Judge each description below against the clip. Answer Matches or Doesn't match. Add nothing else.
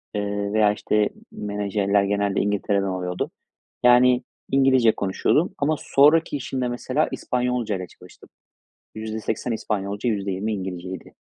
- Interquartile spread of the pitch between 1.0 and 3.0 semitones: Doesn't match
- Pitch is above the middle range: Doesn't match